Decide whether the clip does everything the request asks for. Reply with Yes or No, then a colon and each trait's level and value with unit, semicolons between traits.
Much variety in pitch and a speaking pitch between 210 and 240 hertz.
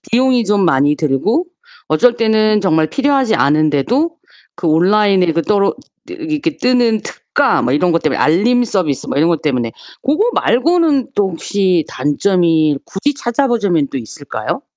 No: wide, 7.7 semitones; high, 200 Hz